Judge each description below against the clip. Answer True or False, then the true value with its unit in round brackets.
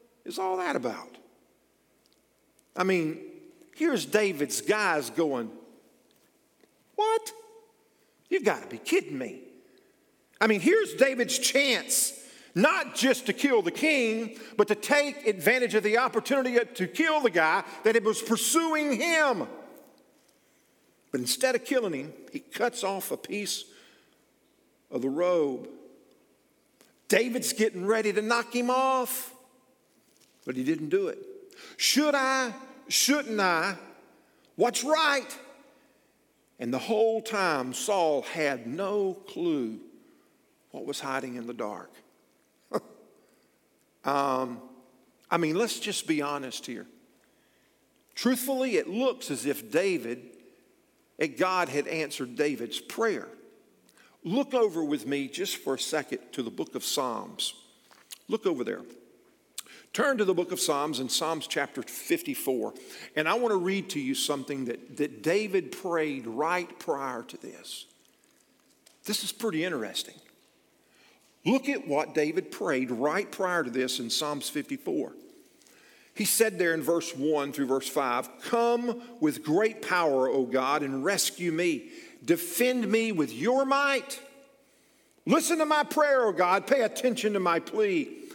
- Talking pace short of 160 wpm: True (135 wpm)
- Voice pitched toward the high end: True (235 Hz)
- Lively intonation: True (8.4 semitones)